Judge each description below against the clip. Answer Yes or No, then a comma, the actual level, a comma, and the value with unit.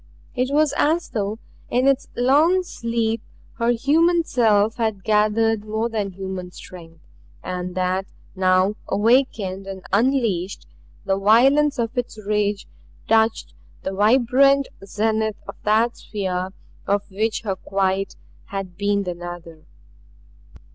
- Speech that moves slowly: Yes, slow, 125 wpm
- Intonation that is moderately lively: Yes, average, 3.9 semitones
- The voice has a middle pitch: No, high, 215 Hz